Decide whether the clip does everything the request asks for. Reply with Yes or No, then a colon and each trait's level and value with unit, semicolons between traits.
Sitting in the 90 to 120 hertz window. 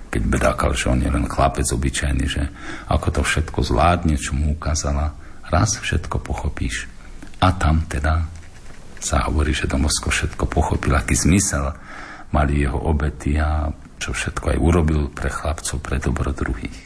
No: very low, 75 Hz